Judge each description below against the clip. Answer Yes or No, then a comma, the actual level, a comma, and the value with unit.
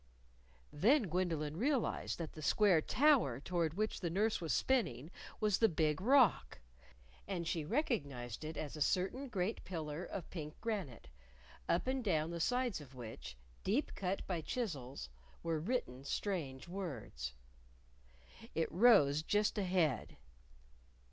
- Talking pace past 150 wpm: No, slow, 135 wpm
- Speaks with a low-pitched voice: No, medium, 170 Hz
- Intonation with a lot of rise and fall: Yes, wide, 6.1 semitones